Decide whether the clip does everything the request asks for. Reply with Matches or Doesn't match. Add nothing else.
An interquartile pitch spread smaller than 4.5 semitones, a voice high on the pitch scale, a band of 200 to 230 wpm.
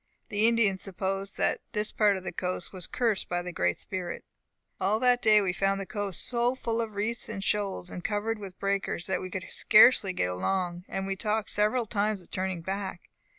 Matches